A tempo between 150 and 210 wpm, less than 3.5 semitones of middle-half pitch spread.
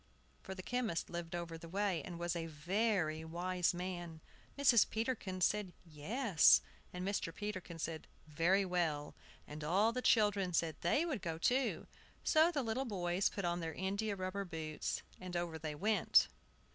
No: average, 165 wpm; average, 3.9 semitones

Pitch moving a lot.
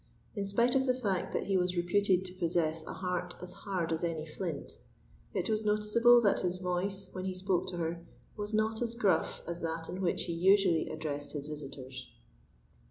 No: average, 3.3 semitones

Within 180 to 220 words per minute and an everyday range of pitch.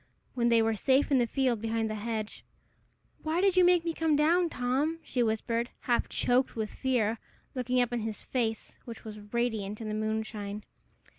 Yes: average, 190 wpm; average, 3.3 semitones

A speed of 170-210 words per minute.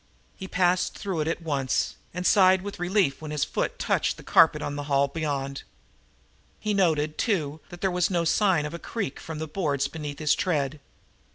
Yes: average, 195 wpm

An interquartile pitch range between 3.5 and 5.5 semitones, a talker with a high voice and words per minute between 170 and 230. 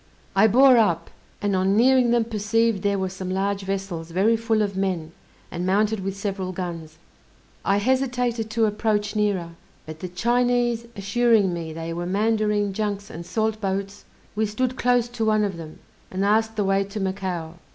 No: average, 2.9 semitones; high, 205 Hz; average, 175 wpm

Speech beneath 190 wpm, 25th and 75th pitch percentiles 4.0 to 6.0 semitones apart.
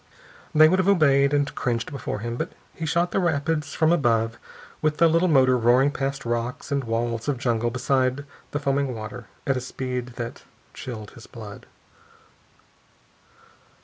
No: average, 160 wpm; average, 3.6 semitones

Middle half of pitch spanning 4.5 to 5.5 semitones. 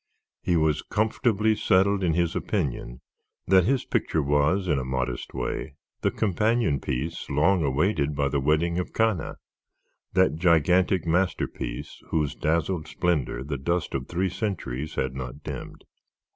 Yes: average, 4.8 semitones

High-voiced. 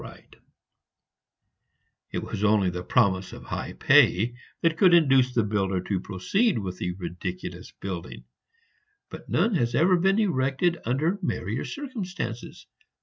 No: low, 120 Hz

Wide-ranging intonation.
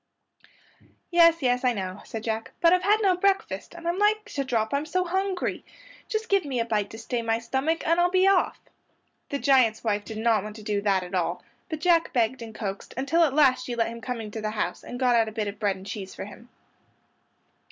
Yes: wide, 7.6 semitones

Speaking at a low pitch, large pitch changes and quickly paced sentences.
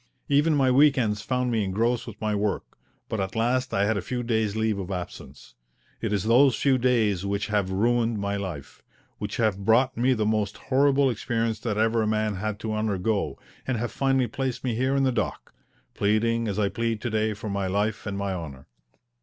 No: low, 110 Hz; average, 3.2 semitones; fast, 210 wpm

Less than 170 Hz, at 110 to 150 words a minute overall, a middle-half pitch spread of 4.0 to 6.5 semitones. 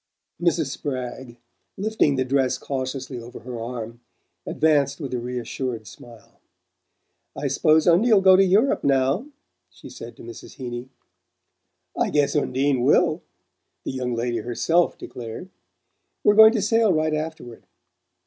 Yes: low, 135 Hz; slow, 135 wpm; average, 5.2 semitones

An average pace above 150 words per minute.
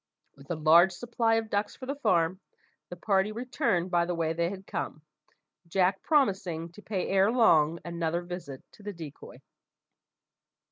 Yes: average, 160 wpm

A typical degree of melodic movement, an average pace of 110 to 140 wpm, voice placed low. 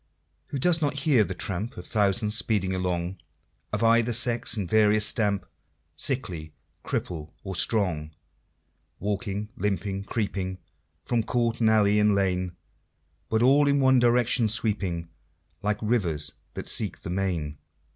Yes: average, 3.9 semitones; slow, 135 wpm; low, 105 Hz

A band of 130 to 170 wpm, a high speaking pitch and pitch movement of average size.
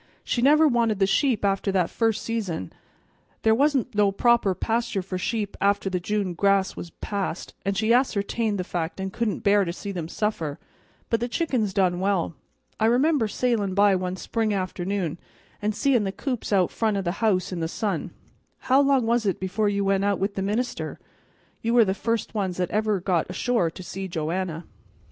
No: average, 195 wpm; high, 200 Hz; average, 3.4 semitones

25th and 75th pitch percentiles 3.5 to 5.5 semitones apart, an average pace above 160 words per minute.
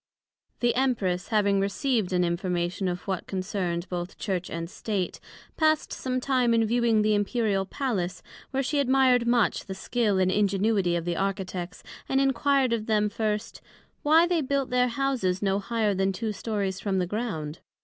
Yes: average, 4.7 semitones; average, 170 wpm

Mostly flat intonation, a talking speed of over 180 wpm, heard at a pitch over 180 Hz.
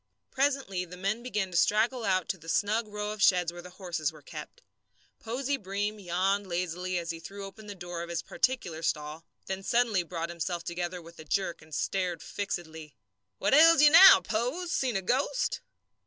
No: average, 4.2 semitones; average, 190 wpm; high, 190 Hz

